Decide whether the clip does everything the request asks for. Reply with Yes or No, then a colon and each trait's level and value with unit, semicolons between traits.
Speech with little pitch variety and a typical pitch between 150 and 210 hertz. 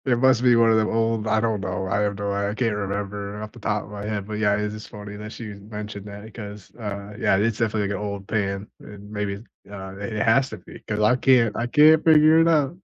No: narrow, 2.1 semitones; low, 105 Hz